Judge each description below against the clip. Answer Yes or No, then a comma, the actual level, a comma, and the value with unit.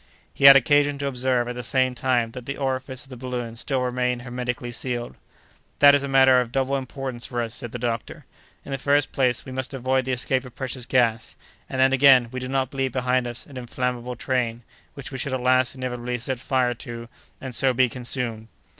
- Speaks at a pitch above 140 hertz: No, low, 125 Hz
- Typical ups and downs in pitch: No, narrow, 1.5 semitones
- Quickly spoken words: Yes, fast, 215 wpm